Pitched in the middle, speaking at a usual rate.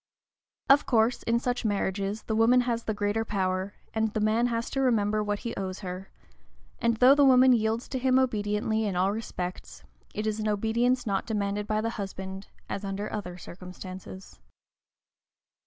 No: high, 215 Hz; average, 170 wpm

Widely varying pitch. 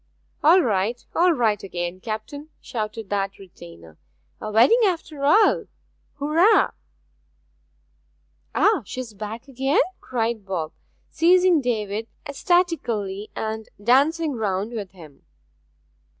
Yes: wide, 6.7 semitones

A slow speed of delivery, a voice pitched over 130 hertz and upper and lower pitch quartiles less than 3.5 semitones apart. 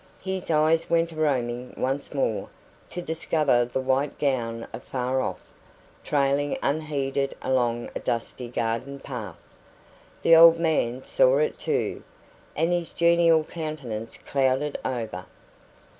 No: slow, 125 wpm; medium, 140 Hz; average, 4.7 semitones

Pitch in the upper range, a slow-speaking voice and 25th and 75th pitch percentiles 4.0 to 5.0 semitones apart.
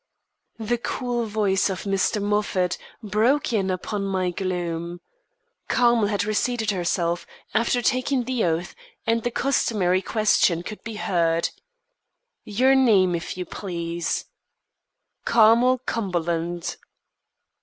Yes: high, 205 Hz; slow, 110 wpm; average, 4.5 semitones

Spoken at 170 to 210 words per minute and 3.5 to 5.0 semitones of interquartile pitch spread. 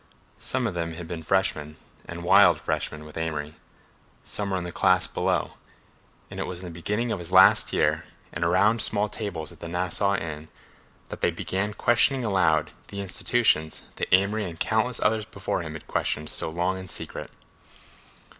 Yes: average, 180 wpm; average, 4.1 semitones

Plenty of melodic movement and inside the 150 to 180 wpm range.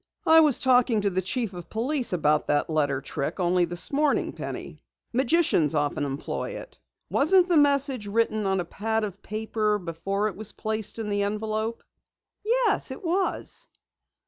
Yes: wide, 6.4 semitones; average, 165 wpm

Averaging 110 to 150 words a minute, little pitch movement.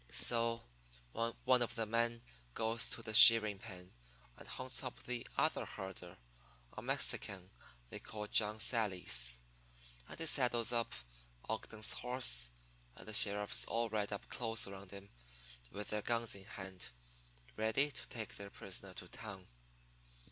No: average, 140 wpm; average, 3.0 semitones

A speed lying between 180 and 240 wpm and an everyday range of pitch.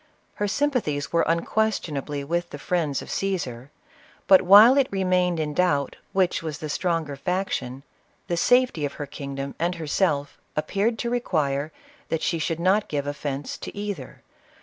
No: average, 160 wpm; average, 5.0 semitones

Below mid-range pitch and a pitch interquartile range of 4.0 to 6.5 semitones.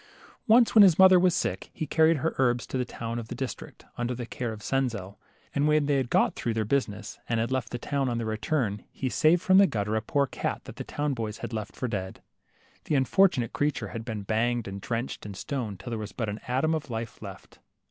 Yes: low, 120 Hz; average, 4.7 semitones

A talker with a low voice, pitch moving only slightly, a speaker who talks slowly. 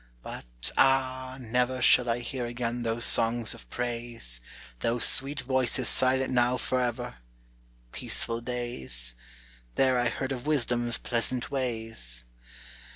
Yes: low, 120 Hz; narrow, 1.8 semitones; slow, 120 wpm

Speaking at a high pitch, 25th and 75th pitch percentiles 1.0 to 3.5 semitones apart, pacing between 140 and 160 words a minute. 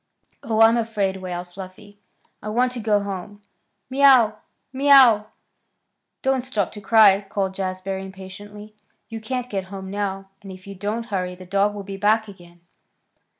Yes: high, 205 Hz; average, 2.7 semitones; average, 155 wpm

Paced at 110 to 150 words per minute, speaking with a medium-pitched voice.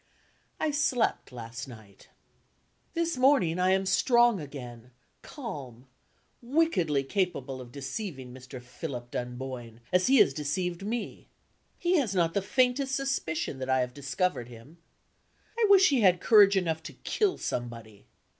Yes: average, 140 wpm; medium, 165 Hz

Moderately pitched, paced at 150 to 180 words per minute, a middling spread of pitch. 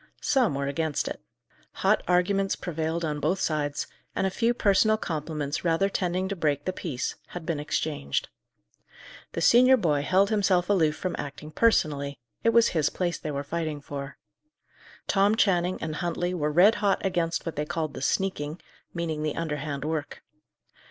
Yes: medium, 165 Hz; average, 165 wpm; average, 4.1 semitones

